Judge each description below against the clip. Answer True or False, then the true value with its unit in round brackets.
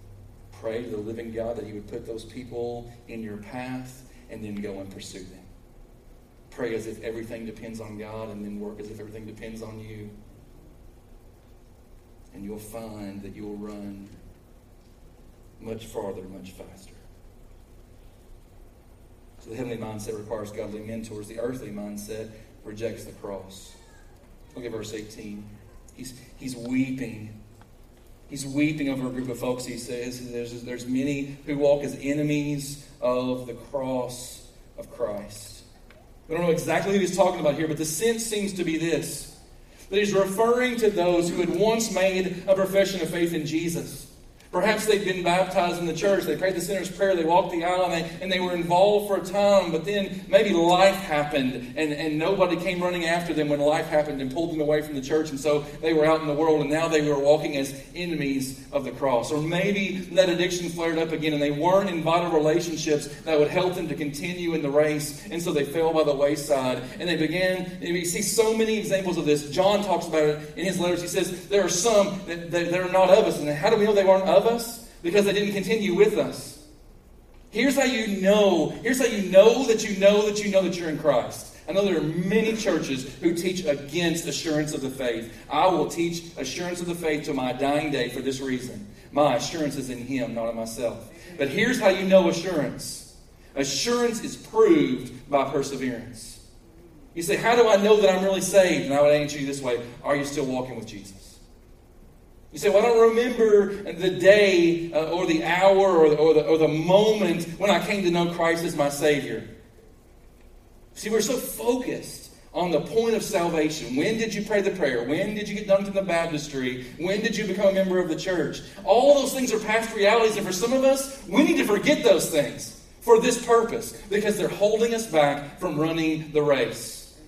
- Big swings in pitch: True (7.8 semitones)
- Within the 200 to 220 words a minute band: True (205 wpm)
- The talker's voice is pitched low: False (155 Hz)